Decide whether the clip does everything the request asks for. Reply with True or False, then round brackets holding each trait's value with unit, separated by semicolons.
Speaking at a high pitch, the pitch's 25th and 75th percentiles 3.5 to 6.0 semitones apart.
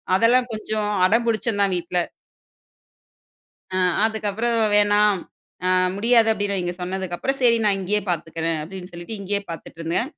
True (205 Hz; 3.8 semitones)